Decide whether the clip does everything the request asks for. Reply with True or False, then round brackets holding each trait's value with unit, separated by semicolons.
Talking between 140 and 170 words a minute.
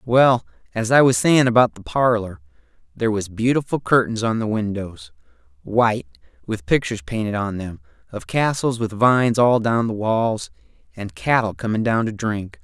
True (165 wpm)